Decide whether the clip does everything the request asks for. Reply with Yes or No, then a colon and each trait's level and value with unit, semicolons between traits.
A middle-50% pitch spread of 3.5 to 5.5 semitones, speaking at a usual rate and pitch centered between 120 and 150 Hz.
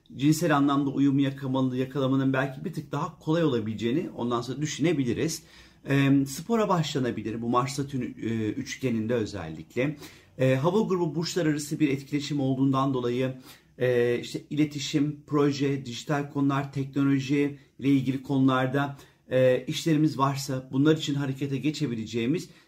No: narrow, 2.4 semitones; average, 125 wpm; medium, 140 Hz